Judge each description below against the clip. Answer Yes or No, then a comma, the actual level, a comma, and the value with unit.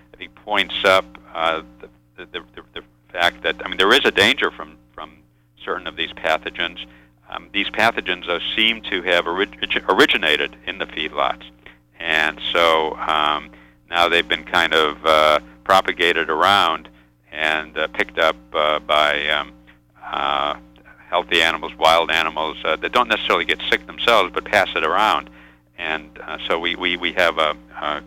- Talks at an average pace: Yes, average, 165 wpm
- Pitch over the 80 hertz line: No, very low, 75 Hz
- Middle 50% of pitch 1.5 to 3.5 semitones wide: No, average, 4.6 semitones